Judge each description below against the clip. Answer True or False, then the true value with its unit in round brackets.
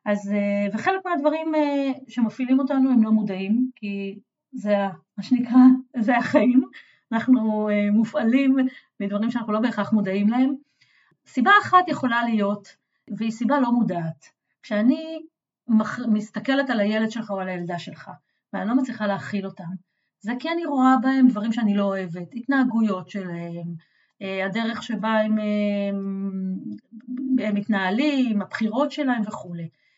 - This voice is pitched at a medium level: False (220 Hz)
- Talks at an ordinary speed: True (130 wpm)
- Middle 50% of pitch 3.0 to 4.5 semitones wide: True (4.2 semitones)